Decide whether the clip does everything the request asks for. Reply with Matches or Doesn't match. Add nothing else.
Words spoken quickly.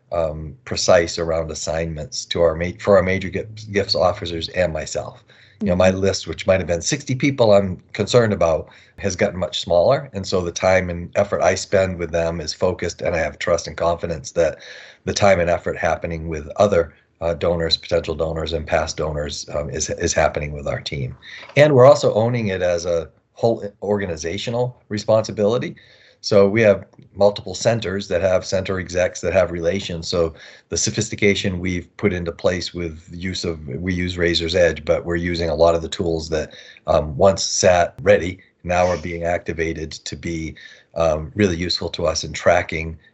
Doesn't match